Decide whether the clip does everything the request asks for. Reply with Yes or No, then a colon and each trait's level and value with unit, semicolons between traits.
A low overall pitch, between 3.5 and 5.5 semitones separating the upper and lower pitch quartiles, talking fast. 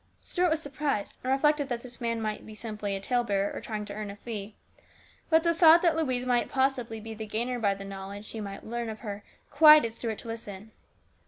No: high, 230 Hz; average, 4.2 semitones; fast, 215 wpm